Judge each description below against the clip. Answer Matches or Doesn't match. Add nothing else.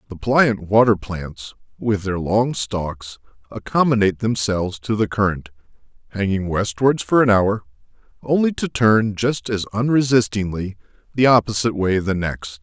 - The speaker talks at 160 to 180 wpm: Doesn't match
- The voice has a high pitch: Doesn't match